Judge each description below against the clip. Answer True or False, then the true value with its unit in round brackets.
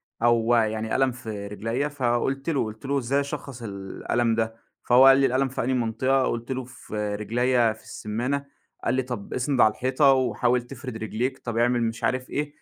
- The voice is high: False (120 Hz)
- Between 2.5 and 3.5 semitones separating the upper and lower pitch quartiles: True (2.8 semitones)